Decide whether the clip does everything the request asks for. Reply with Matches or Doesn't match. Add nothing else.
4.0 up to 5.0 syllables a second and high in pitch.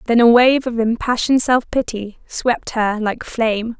Matches